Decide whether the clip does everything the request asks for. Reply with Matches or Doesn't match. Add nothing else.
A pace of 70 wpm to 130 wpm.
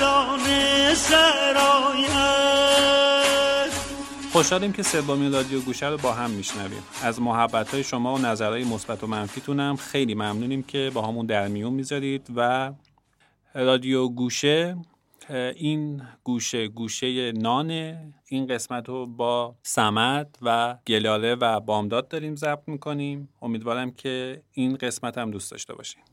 Matches